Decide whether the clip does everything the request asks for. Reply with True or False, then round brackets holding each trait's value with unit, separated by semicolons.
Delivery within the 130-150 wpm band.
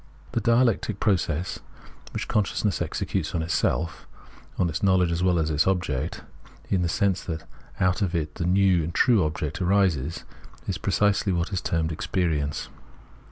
False (170 wpm)